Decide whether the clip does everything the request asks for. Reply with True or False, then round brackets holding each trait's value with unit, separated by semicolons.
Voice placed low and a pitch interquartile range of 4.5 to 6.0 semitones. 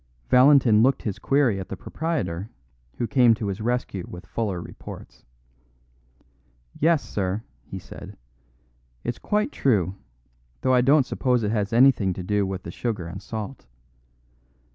True (110 Hz; 4.9 semitones)